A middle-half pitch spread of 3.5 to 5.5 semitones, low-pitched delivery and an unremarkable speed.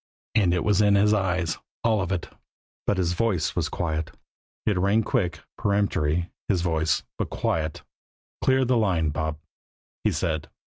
Yes: average, 4.2 semitones; very low, 90 Hz; average, 155 wpm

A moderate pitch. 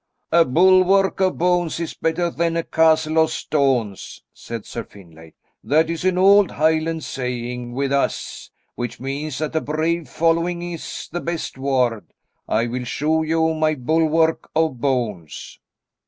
Yes: medium, 155 Hz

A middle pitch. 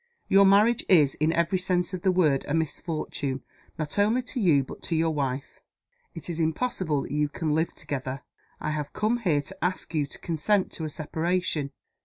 Yes: medium, 160 Hz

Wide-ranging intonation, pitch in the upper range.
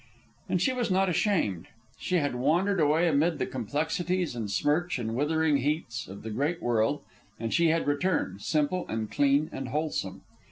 No: wide, 5.7 semitones; medium, 150 Hz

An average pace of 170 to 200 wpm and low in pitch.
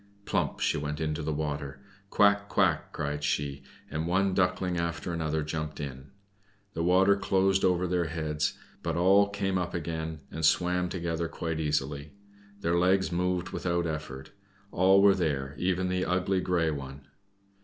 No: average, 155 wpm; very low, 85 Hz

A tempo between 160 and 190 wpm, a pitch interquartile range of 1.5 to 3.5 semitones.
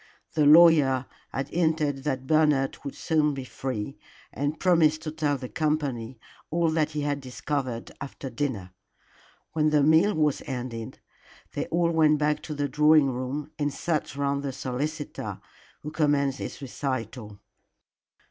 No: average, 150 wpm; narrow, 2.6 semitones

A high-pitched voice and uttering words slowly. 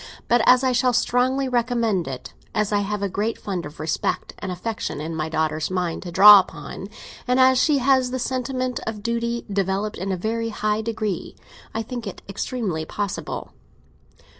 No: high, 215 Hz; average, 180 wpm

